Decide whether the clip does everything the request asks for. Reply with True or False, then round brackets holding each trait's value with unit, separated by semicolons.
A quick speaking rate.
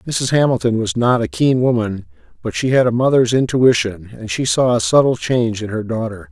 True (210 wpm)